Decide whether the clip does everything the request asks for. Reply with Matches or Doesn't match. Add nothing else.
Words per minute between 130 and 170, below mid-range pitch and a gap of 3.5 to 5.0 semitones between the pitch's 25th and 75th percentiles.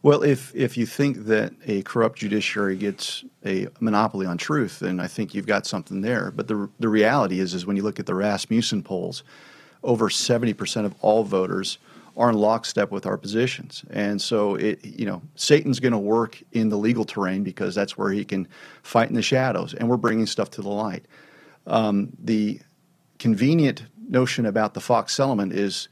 Doesn't match